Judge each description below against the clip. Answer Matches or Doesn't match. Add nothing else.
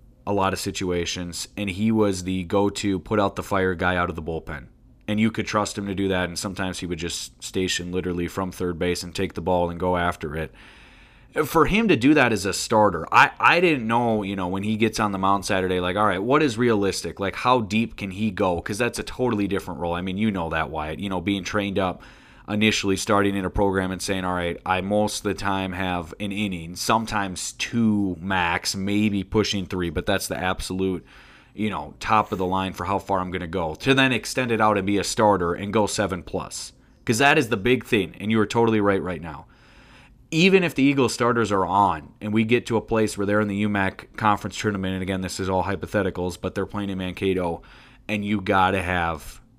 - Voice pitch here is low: Matches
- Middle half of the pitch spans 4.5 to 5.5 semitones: Doesn't match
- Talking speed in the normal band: Doesn't match